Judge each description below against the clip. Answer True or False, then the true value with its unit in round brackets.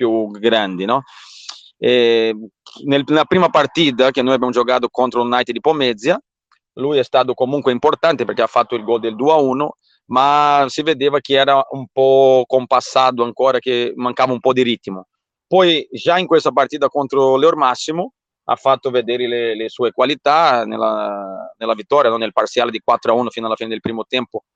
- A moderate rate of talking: False (180 wpm)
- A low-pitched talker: True (130 Hz)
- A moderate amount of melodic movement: True (3.3 semitones)